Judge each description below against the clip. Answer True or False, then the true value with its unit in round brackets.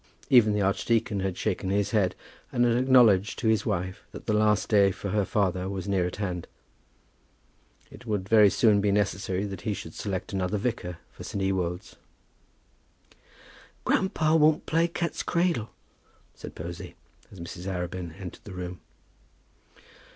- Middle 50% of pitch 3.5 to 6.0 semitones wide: False (3.0 semitones)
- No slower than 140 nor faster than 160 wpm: True (155 wpm)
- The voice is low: True (100 Hz)